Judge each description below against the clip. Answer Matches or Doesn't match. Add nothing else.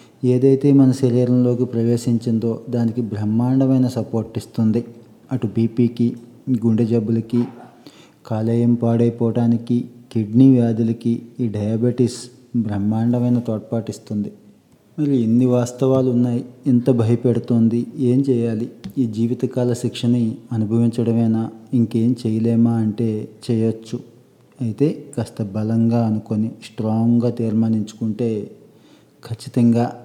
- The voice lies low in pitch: Matches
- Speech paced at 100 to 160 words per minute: Doesn't match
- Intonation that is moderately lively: Doesn't match